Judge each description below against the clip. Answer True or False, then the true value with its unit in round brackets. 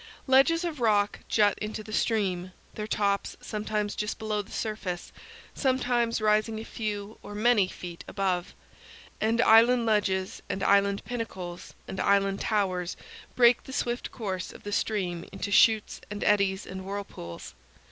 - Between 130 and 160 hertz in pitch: False (210 Hz)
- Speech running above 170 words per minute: False (145 wpm)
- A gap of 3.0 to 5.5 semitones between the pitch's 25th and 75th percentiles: False (2.4 semitones)